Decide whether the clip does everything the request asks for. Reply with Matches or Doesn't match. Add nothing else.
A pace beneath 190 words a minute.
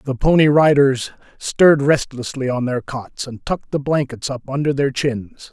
Matches